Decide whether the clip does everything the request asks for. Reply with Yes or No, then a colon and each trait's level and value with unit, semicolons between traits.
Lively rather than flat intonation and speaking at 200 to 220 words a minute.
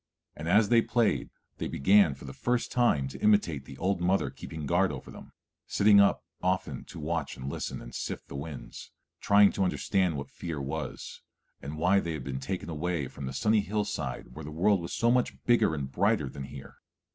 Yes: wide, 6.3 semitones; fast, 205 wpm